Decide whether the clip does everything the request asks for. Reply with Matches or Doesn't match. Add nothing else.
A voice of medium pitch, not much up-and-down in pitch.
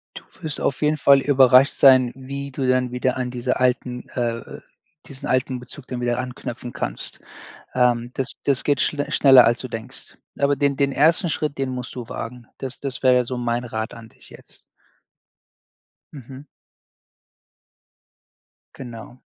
Doesn't match